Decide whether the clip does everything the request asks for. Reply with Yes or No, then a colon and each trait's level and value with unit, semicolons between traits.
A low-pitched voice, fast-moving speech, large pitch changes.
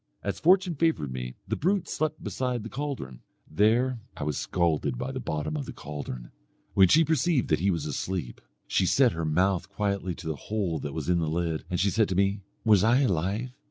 Yes: very low, 95 Hz; fast, 210 wpm; wide, 7.7 semitones